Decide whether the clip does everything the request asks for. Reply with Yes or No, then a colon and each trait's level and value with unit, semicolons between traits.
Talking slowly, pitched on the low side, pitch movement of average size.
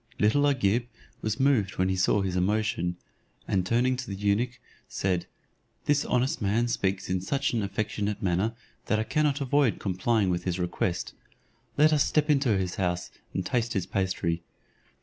No: average, 170 wpm; low, 105 Hz; average, 5.0 semitones